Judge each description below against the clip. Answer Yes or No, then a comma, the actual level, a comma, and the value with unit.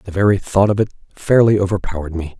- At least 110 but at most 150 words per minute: No, average, 200 wpm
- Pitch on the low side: Yes, very low, 95 Hz